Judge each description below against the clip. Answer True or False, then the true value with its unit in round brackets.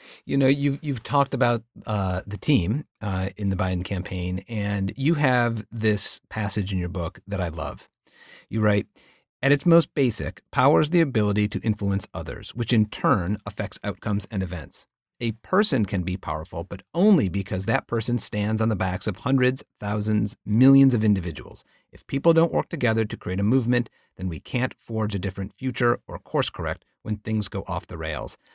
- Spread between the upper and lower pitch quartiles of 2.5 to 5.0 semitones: True (4.0 semitones)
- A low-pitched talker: True (105 Hz)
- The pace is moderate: True (190 wpm)